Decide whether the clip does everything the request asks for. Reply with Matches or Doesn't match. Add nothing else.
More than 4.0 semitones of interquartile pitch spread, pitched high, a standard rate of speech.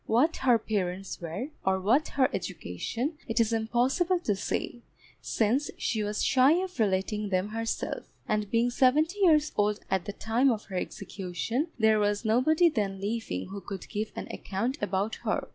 Matches